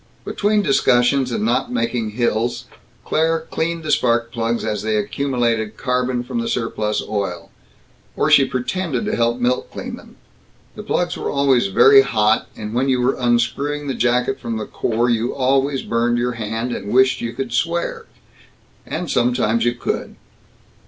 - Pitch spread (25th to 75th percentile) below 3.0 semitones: Yes, narrow, 2.6 semitones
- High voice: No, low, 120 Hz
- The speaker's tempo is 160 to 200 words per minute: Yes, average, 165 wpm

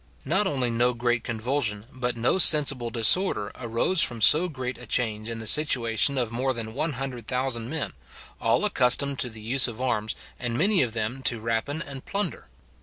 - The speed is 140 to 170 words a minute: No, average, 180 wpm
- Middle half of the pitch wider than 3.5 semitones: No, average, 3.2 semitones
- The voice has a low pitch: Yes, low, 125 Hz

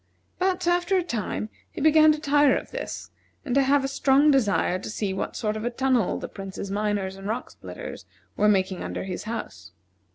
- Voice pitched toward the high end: Yes, high, 240 Hz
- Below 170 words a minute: No, average, 200 wpm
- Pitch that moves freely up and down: Yes, wide, 6.6 semitones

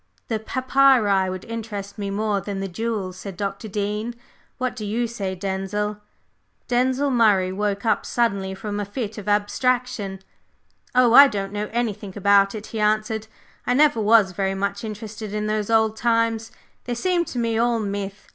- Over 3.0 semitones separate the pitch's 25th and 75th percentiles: No, narrow, 2.5 semitones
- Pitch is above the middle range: Yes, high, 210 Hz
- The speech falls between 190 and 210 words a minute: No, average, 170 wpm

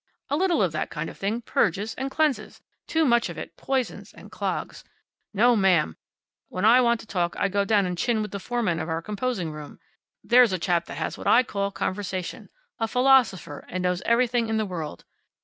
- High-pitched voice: Yes, high, 210 Hz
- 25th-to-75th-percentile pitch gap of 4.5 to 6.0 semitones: Yes, average, 5.0 semitones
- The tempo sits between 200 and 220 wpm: Yes, fast, 205 wpm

